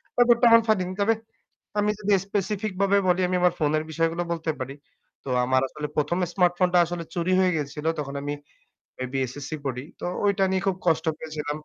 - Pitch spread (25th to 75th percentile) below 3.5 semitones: No, average, 4.5 semitones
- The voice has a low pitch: No, medium, 170 Hz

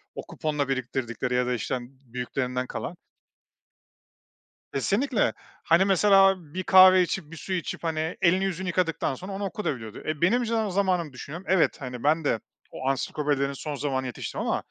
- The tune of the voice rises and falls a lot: Yes, wide, 6.2 semitones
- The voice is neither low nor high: Yes, medium, 160 Hz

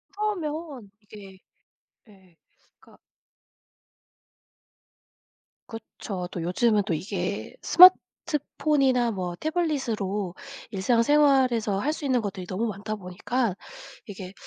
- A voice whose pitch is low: No, high, 215 Hz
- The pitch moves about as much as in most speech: No, wide, 6.3 semitones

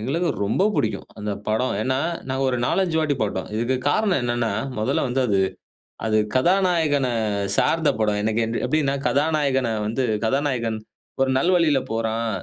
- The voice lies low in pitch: Yes, low, 130 Hz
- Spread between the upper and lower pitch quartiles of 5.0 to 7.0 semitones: Yes, wide, 5.4 semitones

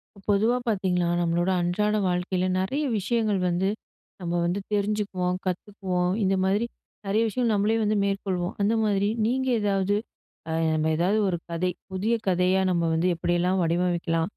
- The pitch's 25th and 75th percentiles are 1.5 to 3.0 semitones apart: Yes, average, 2.7 semitones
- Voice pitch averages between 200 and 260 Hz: No, high, 190 Hz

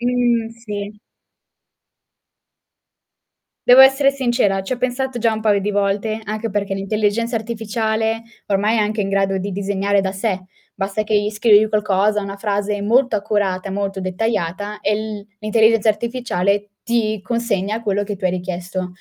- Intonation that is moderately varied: No, narrow, 2.2 semitones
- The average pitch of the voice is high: Yes, high, 210 Hz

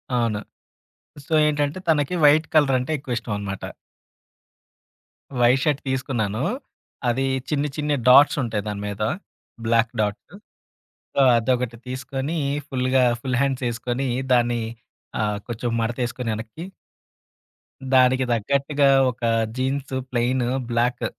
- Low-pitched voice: Yes, low, 125 Hz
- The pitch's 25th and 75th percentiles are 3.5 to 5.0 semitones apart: No, average, 2.9 semitones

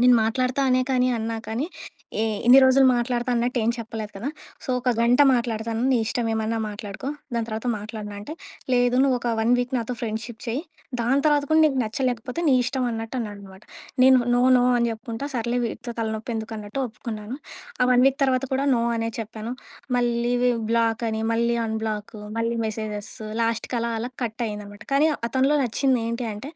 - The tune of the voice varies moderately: No, narrow, 2.3 semitones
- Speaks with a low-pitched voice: No, high, 235 Hz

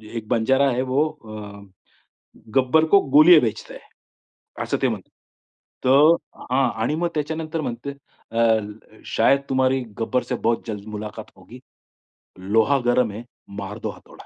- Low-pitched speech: Yes, low, 125 Hz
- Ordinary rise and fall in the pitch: Yes, average, 4.2 semitones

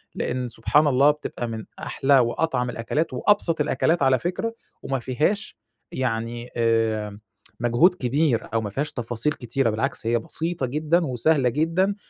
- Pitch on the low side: Yes, low, 130 Hz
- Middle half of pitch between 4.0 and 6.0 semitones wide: Yes, average, 5.1 semitones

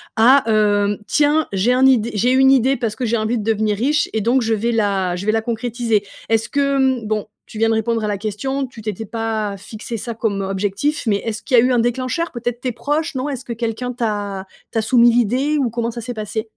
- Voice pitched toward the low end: No, high, 230 Hz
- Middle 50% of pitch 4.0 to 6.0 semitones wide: No, average, 2.8 semitones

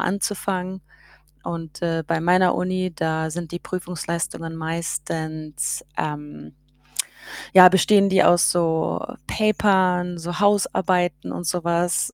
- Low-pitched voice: No, medium, 175 Hz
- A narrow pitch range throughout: Yes, narrow, 2.2 semitones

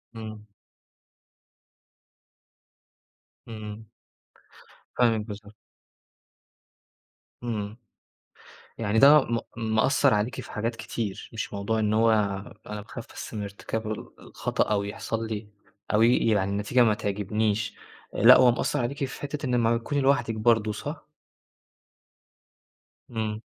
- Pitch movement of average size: No, narrow, 2.0 semitones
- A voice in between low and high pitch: No, low, 110 Hz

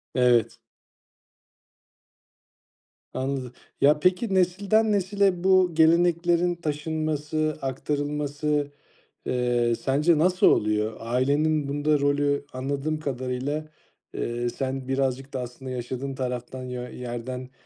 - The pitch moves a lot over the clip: No, average, 3.7 semitones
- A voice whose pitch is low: No, medium, 145 Hz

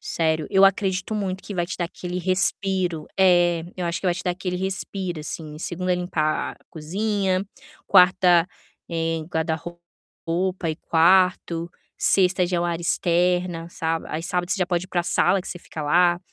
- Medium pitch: Yes, medium, 175 Hz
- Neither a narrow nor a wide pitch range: No, narrow, 1.7 semitones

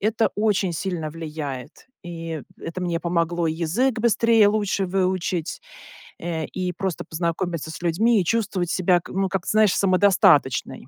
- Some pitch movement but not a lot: Yes, average, 3.2 semitones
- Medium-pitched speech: Yes, medium, 180 Hz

